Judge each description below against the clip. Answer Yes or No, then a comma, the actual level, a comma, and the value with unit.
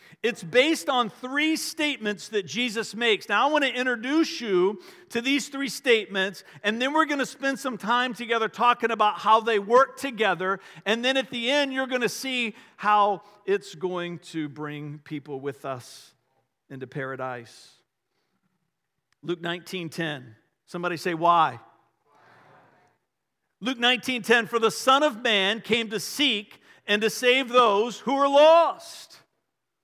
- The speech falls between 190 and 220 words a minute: No, average, 150 wpm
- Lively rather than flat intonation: Yes, wide, 6.5 semitones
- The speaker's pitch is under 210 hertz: No, high, 220 Hz